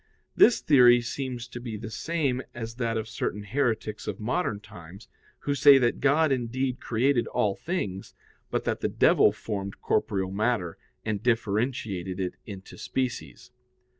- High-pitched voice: No, low, 115 Hz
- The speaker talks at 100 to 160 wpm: Yes, average, 150 wpm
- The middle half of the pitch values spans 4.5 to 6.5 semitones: No, average, 4.1 semitones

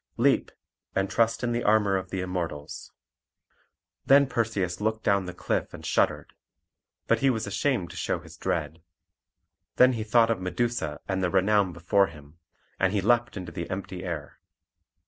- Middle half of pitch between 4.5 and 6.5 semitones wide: No, average, 4.0 semitones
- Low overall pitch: Yes, low, 100 Hz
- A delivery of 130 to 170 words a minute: Yes, average, 165 wpm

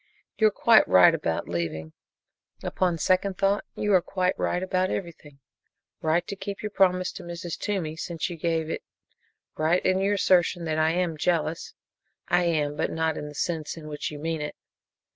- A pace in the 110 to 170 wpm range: No, average, 185 wpm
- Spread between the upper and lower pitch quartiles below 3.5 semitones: Yes, average, 2.9 semitones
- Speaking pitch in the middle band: Yes, medium, 170 Hz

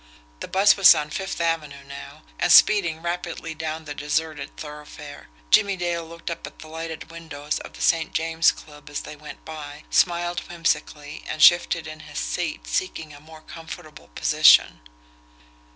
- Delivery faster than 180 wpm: No, average, 165 wpm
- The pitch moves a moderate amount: No, narrow, 2.0 semitones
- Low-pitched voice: No, medium, 160 Hz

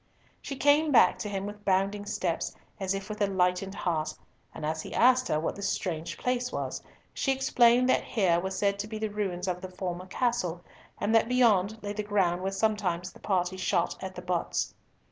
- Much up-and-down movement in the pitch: No, average, 3.3 semitones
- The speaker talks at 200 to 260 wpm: Yes, fast, 205 wpm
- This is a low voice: No, high, 195 Hz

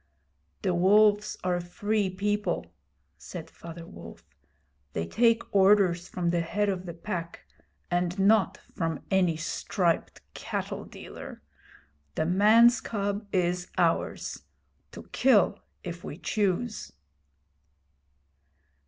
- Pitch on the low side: No, medium, 185 Hz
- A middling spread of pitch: Yes, average, 3.2 semitones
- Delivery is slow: Yes, slow, 110 wpm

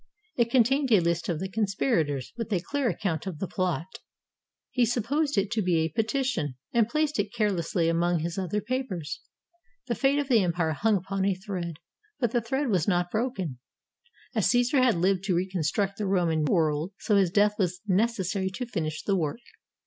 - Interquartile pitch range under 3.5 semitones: No, average, 5.3 semitones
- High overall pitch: Yes, high, 195 Hz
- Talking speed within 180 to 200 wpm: Yes, average, 190 wpm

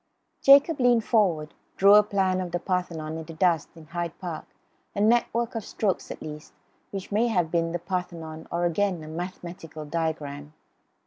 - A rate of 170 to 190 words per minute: Yes, average, 175 wpm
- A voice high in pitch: No, medium, 175 Hz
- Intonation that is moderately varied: Yes, average, 4.0 semitones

